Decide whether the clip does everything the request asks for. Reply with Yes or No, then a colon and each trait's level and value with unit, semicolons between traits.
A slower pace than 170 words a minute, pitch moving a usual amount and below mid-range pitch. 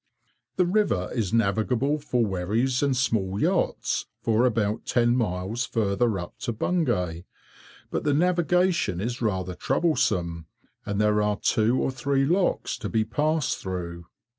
No: average, 140 wpm; wide, 5.7 semitones; low, 115 Hz